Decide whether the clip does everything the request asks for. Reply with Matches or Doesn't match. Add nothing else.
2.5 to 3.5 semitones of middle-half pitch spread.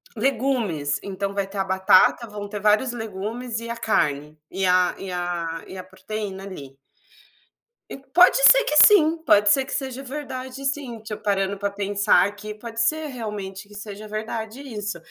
Doesn't match